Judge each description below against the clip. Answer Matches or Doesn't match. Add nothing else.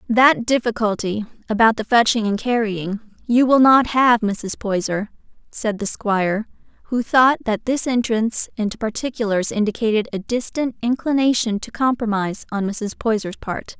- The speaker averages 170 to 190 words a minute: Doesn't match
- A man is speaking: Doesn't match